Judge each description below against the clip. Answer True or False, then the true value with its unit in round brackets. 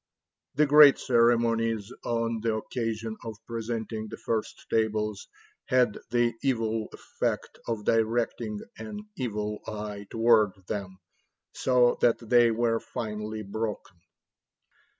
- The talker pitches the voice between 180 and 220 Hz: False (115 Hz)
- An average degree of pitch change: False (1.8 semitones)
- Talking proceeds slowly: True (110 wpm)